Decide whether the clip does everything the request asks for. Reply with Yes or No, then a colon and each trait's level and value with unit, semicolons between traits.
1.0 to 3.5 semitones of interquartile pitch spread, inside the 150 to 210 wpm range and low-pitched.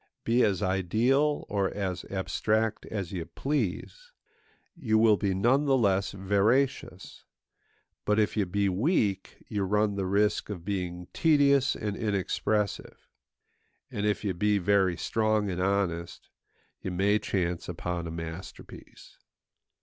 No: average, 2.7 semitones; slow, 135 wpm; low, 100 Hz